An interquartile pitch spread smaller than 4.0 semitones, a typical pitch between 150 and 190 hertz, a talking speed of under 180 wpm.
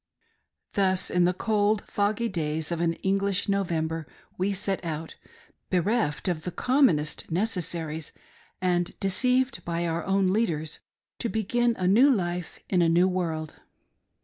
Yes: average, 3.5 semitones; medium, 185 Hz; average, 140 wpm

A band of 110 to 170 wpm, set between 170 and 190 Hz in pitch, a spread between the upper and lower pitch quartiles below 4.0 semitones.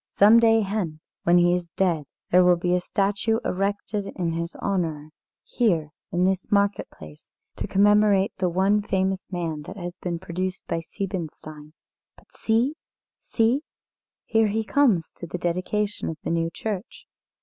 Yes: average, 160 wpm; medium, 185 Hz; average, 3.4 semitones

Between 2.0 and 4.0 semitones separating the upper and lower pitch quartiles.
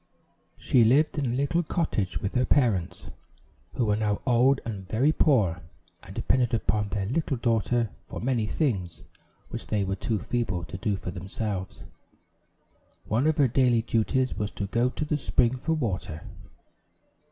No: average, 4.6 semitones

